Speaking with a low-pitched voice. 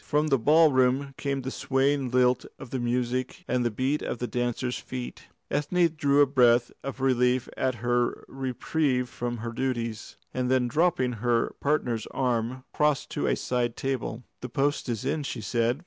Yes: low, 130 Hz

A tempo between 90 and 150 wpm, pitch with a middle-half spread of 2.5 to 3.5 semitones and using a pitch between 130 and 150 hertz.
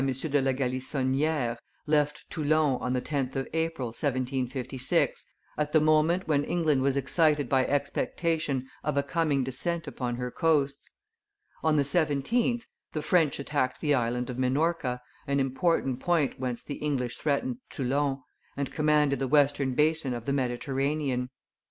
Yes: average, 145 wpm; average, 2.9 semitones; medium, 140 Hz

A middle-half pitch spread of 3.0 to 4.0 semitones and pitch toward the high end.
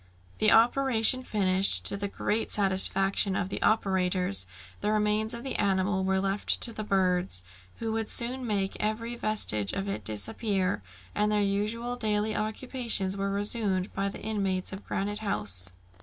No: narrow, 2.4 semitones; high, 205 Hz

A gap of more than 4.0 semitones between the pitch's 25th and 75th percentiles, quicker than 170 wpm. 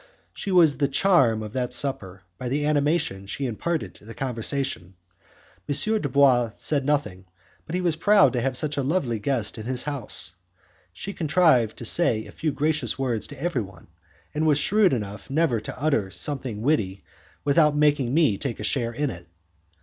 Yes: average, 4.9 semitones; average, 180 wpm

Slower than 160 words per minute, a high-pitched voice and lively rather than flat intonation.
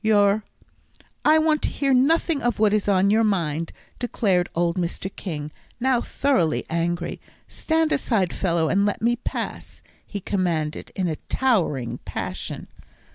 Yes: average, 150 wpm; high, 200 Hz; wide, 6.0 semitones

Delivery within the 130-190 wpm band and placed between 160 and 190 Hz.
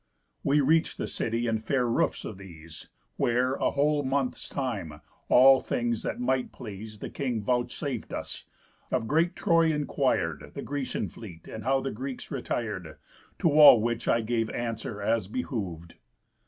No: average, 155 wpm; low, 120 Hz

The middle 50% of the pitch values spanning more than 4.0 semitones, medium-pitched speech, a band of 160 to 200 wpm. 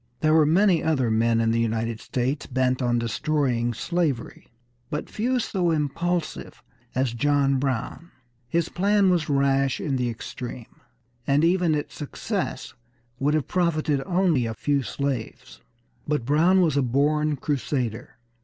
No: average, 4.7 semitones; medium, 145 Hz; average, 145 wpm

